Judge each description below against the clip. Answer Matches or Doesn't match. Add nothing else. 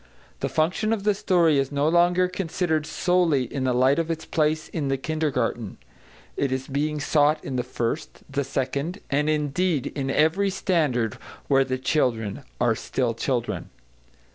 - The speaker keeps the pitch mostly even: Doesn't match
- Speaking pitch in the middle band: Matches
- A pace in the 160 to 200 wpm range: Matches